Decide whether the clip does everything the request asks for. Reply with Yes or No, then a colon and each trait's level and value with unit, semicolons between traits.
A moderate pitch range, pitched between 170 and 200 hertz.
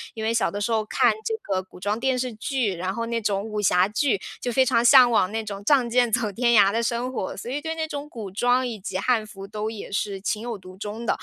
No: average, 3.4 semitones; high, 225 Hz